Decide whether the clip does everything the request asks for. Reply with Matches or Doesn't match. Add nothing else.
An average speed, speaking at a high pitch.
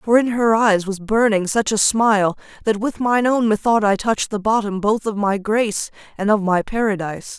Doesn't match